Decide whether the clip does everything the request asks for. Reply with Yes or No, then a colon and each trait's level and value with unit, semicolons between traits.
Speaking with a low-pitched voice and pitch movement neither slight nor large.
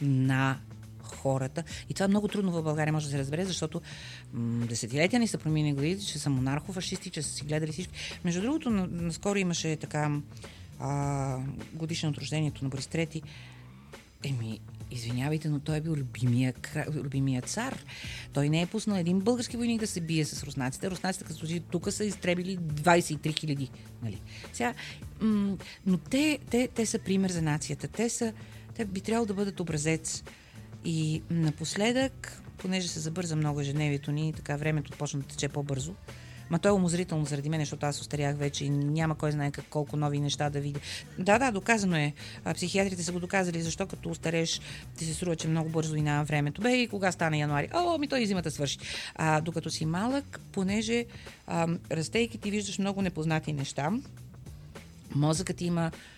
No: medium, 155 Hz; average, 4.7 semitones